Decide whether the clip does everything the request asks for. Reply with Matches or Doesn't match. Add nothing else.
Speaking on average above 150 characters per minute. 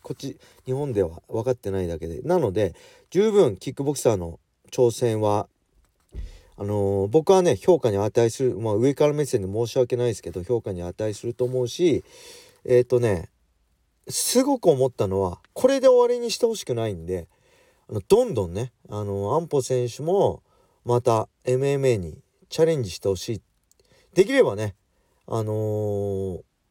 Matches